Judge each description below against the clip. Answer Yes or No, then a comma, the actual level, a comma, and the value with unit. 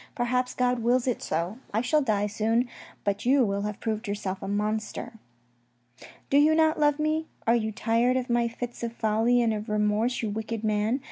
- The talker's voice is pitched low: No, high, 230 Hz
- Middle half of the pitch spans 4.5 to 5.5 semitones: No, average, 2.9 semitones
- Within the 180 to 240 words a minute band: Yes, average, 200 wpm